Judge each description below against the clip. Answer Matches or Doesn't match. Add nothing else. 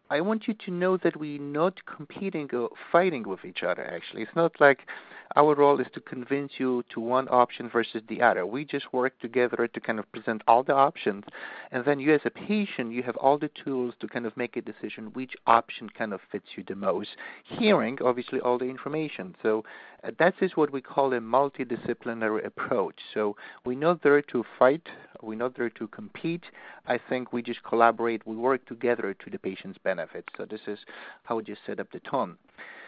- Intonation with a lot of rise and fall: Doesn't match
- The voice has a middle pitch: Doesn't match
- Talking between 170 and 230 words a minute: Matches